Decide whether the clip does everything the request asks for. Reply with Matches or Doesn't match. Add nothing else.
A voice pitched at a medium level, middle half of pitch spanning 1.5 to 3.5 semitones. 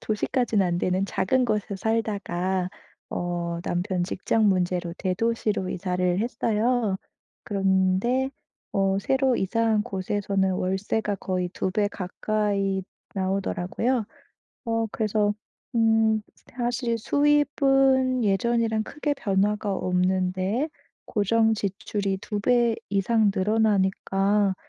Doesn't match